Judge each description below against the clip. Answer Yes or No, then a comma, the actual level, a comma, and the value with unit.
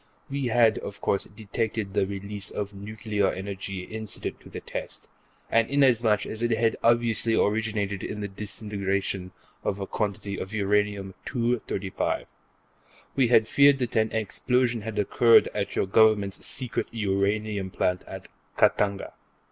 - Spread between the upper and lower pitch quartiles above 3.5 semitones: No, narrow, 2.4 semitones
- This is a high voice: No, low, 105 Hz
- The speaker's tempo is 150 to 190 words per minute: No, average, 140 wpm